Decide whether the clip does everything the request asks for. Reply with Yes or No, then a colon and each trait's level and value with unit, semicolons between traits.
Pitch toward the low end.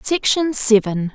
No: high, 240 Hz